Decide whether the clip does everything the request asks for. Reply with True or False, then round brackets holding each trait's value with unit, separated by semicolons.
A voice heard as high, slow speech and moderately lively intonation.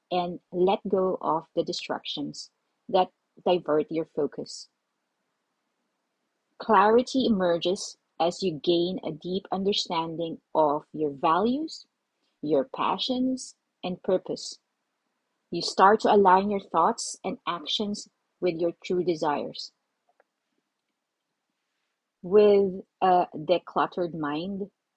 False (180 Hz; 100 wpm; 3.1 semitones)